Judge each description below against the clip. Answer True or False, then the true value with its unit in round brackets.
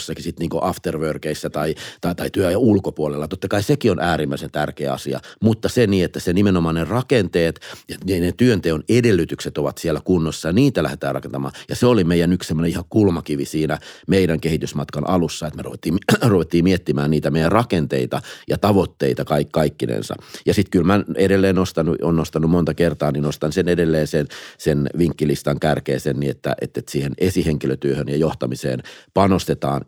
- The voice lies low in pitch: True (80 Hz)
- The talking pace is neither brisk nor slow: False (175 wpm)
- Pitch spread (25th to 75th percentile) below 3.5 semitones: False (3.8 semitones)